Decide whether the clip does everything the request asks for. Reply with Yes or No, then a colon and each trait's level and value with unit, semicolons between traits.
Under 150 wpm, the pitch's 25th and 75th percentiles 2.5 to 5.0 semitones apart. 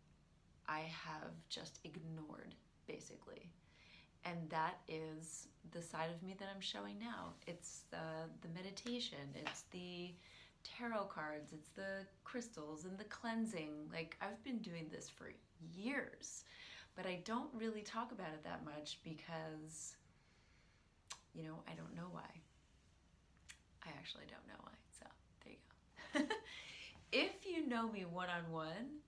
No: average, 140 wpm; wide, 5.5 semitones